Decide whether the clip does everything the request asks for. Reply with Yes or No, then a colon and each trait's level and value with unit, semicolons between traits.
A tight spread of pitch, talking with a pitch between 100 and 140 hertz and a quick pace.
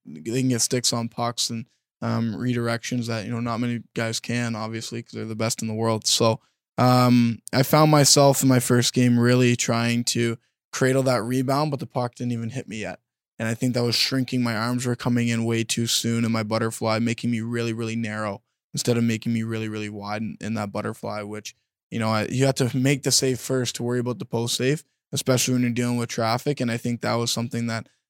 Yes: narrow, 1.7 semitones; low, 120 Hz; fast, 235 wpm